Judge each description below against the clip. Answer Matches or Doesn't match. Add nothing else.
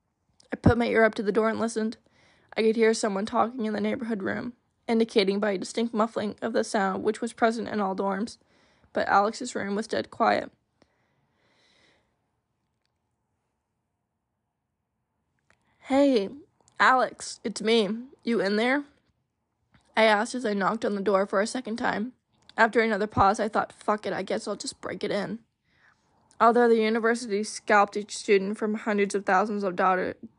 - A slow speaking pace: Doesn't match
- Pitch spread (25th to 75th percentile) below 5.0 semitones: Matches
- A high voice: Matches